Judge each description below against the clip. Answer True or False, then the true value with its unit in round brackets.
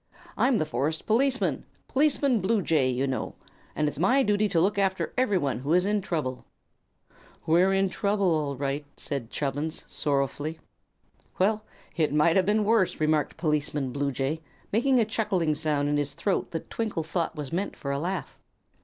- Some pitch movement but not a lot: False (6.0 semitones)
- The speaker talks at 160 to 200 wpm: True (165 wpm)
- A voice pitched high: False (165 Hz)